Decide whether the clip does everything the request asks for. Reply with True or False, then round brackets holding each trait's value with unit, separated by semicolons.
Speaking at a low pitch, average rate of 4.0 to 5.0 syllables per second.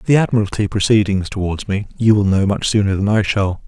False (100 Hz; 5.7 syllables/s)